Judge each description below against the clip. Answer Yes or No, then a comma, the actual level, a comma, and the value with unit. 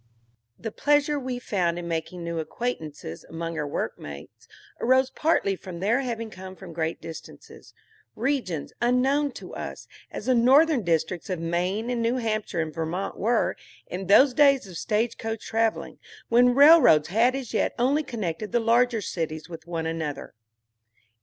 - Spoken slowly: No, average, 160 wpm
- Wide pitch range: Yes, wide, 6.8 semitones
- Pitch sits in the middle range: No, high, 215 Hz